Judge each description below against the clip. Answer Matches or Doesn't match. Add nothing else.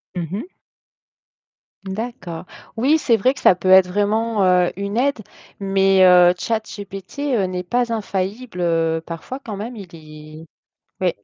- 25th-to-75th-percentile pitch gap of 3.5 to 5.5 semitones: Matches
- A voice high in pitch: Matches